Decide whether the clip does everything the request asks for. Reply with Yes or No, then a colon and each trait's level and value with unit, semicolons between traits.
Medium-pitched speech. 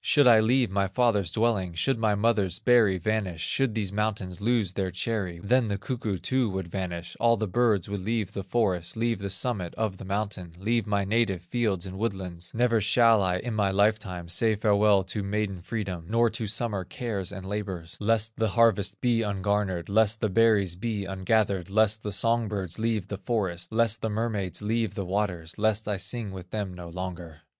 No: low, 105 Hz